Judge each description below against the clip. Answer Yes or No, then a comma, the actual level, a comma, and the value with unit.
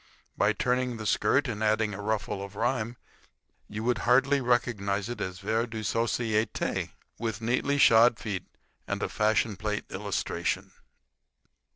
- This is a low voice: Yes, low, 110 Hz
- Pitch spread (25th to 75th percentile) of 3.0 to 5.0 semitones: No, narrow, 2.5 semitones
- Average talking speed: Yes, average, 145 wpm